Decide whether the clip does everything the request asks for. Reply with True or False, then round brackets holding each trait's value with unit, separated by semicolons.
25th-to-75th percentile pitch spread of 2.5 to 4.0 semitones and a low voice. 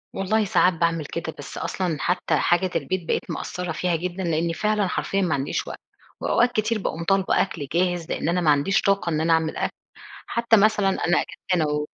False (3.1 semitones; 180 Hz)